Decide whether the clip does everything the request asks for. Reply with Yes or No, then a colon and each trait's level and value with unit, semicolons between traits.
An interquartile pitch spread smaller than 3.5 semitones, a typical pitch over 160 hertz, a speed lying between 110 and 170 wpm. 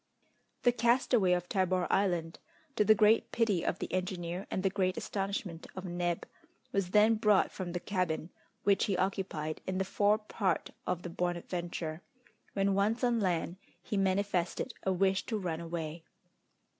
Yes: narrow, 2.6 semitones; medium, 185 Hz; average, 160 wpm